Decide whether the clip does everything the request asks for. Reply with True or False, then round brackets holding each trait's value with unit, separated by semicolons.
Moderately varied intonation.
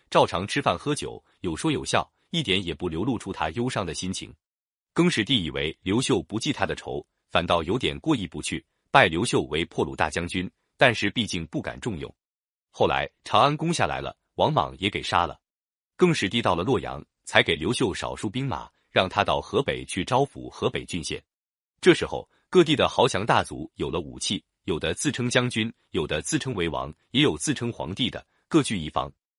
False (8.8 semitones)